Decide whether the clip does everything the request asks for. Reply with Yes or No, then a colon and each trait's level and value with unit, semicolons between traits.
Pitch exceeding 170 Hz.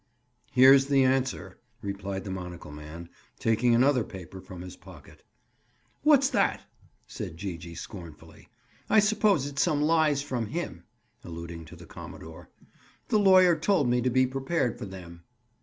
No: low, 120 Hz